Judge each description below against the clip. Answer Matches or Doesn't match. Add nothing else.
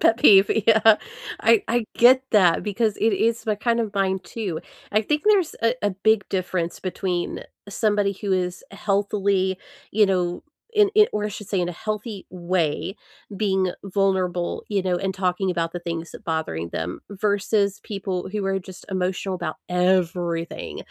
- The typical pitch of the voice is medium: Doesn't match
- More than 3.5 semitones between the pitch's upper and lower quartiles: Doesn't match